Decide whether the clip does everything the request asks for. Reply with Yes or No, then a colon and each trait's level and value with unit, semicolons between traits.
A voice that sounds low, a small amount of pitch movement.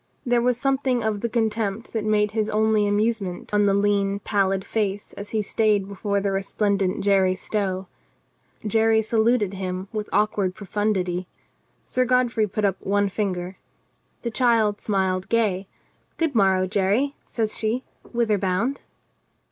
No: high, 210 Hz; narrow, 2.3 semitones